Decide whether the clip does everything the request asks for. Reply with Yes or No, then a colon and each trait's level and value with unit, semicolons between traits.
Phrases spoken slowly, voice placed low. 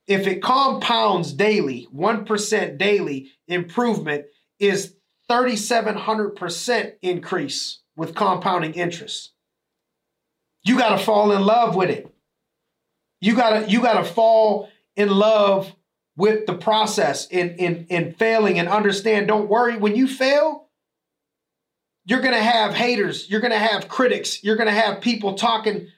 No: slow, 130 wpm; high, 210 Hz